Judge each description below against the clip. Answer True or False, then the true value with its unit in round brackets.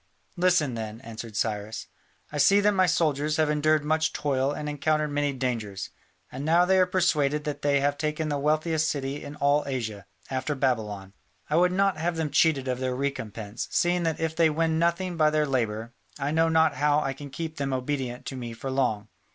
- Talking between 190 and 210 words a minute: True (200 wpm)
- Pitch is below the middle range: False (145 Hz)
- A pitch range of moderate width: True (3.6 semitones)